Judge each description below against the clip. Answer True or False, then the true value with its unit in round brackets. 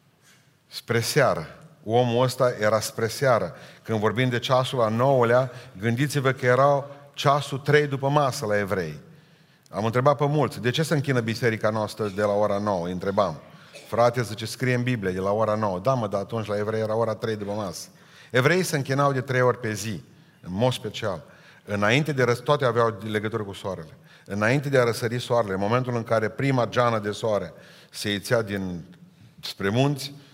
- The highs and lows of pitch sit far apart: False (4.2 semitones)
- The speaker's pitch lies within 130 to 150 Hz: False (120 Hz)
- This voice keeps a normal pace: False (190 wpm)